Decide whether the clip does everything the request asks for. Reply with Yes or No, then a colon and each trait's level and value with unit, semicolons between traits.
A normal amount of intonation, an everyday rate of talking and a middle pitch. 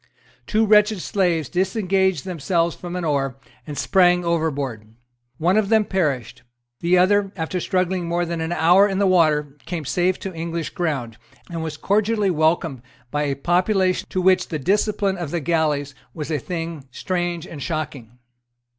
Yes: average, 3.5 semitones; average, 165 wpm; medium, 170 Hz